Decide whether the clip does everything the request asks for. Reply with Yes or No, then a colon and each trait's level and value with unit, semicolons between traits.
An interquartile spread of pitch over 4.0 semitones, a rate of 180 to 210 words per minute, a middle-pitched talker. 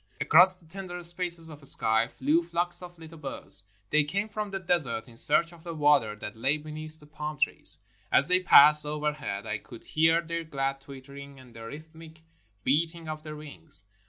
No: average, 3.5 semitones; average, 190 wpm; medium, 155 Hz